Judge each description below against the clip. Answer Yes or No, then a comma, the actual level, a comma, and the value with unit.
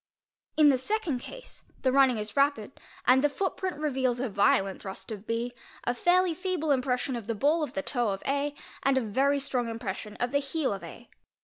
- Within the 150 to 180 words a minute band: No, fast, 205 wpm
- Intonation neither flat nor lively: Yes, average, 4.1 semitones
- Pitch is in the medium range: No, very high, 265 Hz